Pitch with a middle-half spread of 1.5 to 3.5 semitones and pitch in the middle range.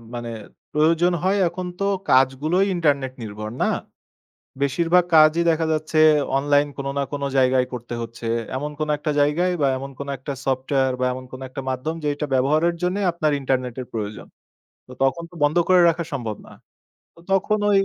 No: average, 4.2 semitones; medium, 145 Hz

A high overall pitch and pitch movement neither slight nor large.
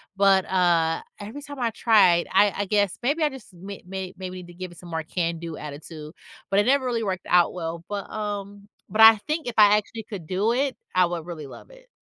Yes: high, 195 Hz; average, 4.2 semitones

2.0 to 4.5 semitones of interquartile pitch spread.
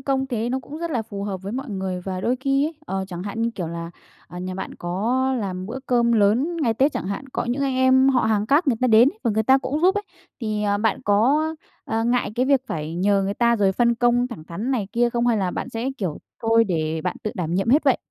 No: average, 5.0 semitones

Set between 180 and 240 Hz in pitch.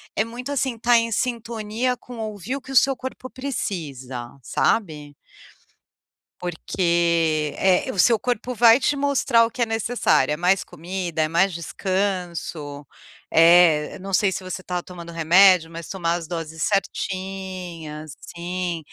Yes: medium, 185 Hz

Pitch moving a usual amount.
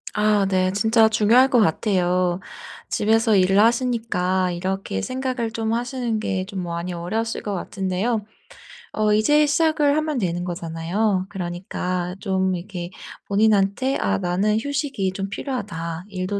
Yes: average, 3.8 semitones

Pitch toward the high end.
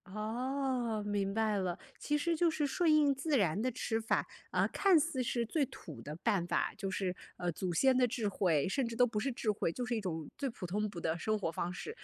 Yes: high, 225 Hz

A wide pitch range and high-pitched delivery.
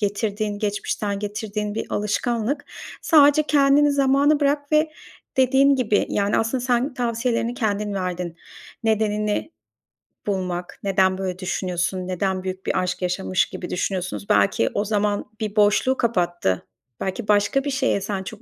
No: average, 4.9 semitones; high, 210 Hz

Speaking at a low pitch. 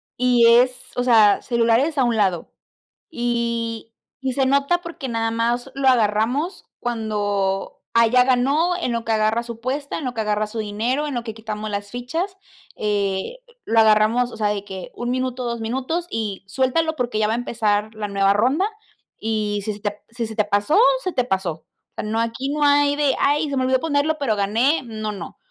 No: high, 235 Hz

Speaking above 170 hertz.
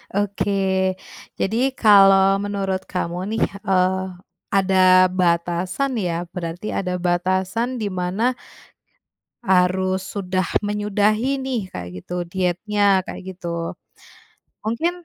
Yes: high, 190 Hz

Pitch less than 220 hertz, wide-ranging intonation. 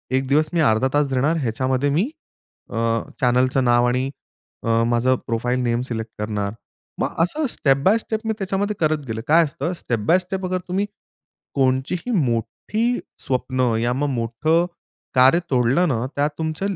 Yes: low, 135 Hz; wide, 5.7 semitones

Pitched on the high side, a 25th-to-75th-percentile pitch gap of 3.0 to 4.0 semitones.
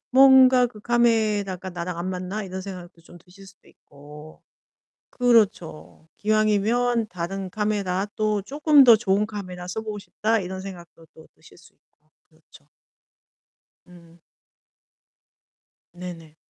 Yes: high, 195 Hz; average, 3.6 semitones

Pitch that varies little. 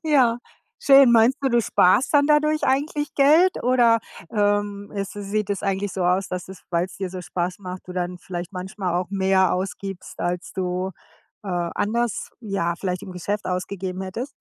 No: average, 4.3 semitones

